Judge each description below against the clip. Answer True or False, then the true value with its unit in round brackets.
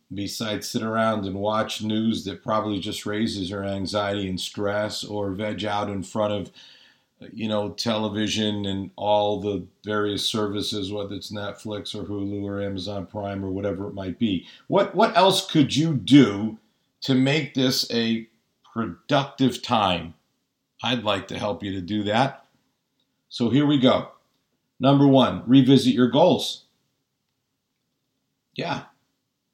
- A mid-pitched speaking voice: False (105 Hz)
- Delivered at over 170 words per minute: False (145 wpm)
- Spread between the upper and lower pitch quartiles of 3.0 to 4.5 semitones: True (3.7 semitones)